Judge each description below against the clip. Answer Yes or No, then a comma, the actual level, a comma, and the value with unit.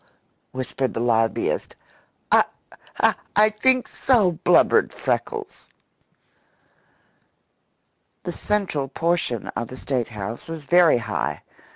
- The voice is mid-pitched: Yes, medium, 145 Hz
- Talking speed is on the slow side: Yes, slow, 95 wpm